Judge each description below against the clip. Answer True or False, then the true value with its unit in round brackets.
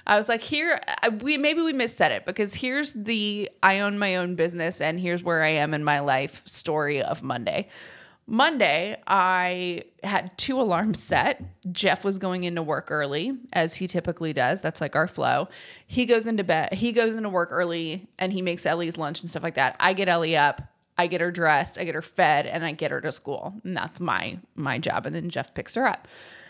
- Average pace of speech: False (215 wpm)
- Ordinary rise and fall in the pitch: True (4.6 semitones)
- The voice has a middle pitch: True (180 Hz)